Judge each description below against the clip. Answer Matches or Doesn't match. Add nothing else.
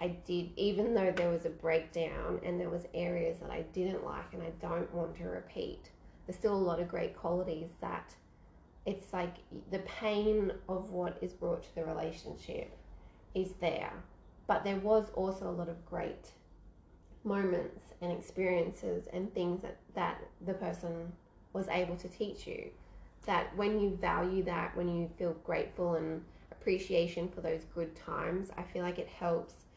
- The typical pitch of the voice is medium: Matches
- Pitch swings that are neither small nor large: Doesn't match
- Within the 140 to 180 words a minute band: Matches